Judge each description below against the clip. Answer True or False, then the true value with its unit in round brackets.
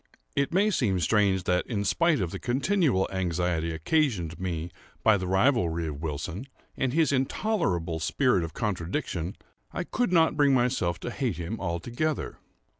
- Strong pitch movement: True (8.3 semitones)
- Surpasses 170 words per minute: False (155 wpm)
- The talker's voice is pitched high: False (100 Hz)